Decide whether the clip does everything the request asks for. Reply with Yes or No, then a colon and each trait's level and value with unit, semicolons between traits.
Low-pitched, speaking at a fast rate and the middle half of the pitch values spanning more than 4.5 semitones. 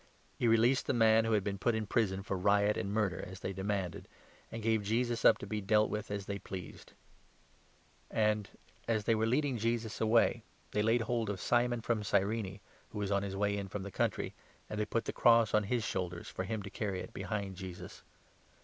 No: low, 105 Hz; fast, 225 wpm; narrow, 2.4 semitones